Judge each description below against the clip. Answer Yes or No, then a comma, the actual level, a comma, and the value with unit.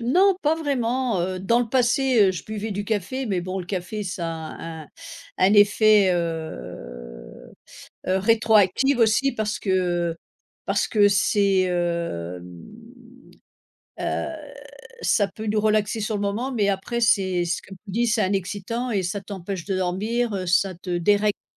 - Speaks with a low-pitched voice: No, high, 200 Hz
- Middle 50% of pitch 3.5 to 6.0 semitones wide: Yes, average, 3.8 semitones